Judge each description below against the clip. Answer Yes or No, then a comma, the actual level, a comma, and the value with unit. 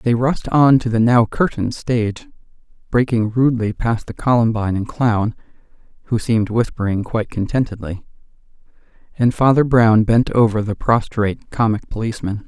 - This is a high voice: No, low, 115 Hz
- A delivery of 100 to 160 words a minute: Yes, average, 140 wpm